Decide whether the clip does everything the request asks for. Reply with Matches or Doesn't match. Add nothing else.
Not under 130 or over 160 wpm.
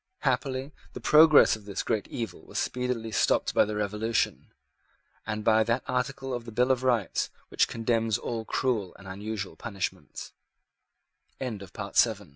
Matches